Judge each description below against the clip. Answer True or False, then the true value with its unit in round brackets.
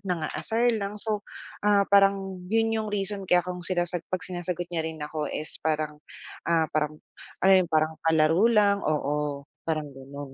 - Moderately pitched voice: True (175 Hz)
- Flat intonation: False (4.3 semitones)